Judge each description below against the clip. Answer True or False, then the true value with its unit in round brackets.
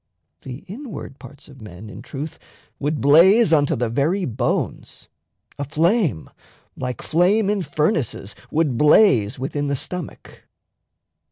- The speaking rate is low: True (125 wpm)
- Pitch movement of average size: False (5.8 semitones)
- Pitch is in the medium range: True (145 Hz)